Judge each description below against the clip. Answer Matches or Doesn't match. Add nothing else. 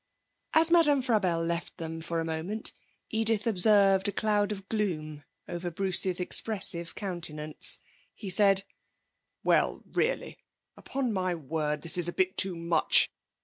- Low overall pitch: Doesn't match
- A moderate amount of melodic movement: Matches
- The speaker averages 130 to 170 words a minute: Matches